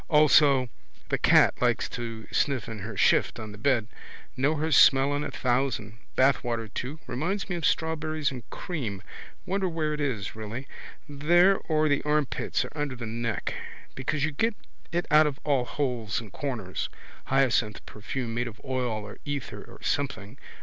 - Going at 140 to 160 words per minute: No, average, 170 wpm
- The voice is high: No, low, 135 Hz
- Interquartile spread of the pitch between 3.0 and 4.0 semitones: No, average, 4.7 semitones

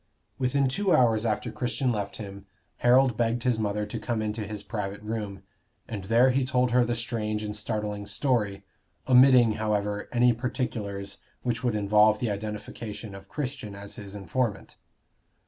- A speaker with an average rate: Yes, average, 160 wpm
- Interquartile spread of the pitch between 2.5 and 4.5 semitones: Yes, average, 3.0 semitones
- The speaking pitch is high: No, low, 110 Hz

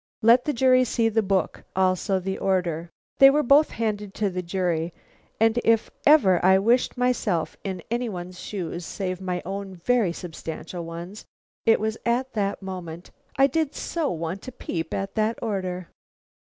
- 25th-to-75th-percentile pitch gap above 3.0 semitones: Yes, average, 4.5 semitones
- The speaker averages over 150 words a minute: Yes, average, 170 wpm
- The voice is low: No, high, 195 Hz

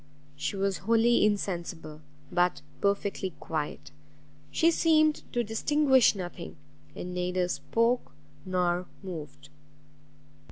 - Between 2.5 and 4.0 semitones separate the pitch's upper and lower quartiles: No, average, 4.6 semitones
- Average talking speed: No, slow, 95 wpm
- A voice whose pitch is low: No, high, 190 Hz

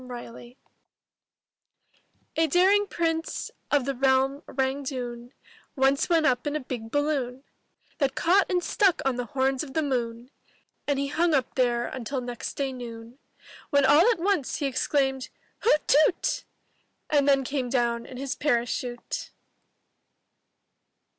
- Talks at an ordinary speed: Yes, average, 155 wpm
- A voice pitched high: Yes, very high, 270 Hz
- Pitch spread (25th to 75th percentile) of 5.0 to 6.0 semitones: No, average, 3.2 semitones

